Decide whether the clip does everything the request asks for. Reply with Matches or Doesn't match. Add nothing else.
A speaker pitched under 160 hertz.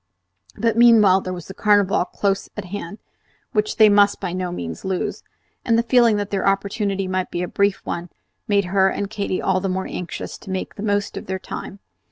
Doesn't match